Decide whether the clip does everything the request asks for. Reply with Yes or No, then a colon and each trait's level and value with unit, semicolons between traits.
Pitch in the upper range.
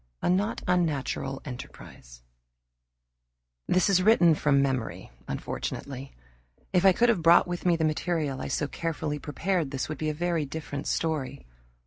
No: medium, 155 Hz